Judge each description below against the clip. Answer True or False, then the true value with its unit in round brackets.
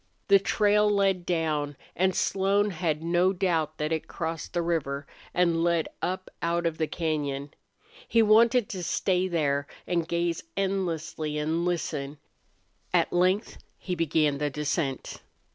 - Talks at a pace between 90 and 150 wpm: True (145 wpm)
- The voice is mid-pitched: True (170 Hz)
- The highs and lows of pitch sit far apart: False (3.4 semitones)